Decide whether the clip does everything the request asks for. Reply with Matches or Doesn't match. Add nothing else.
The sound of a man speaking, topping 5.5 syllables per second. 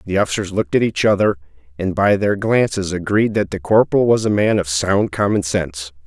Matches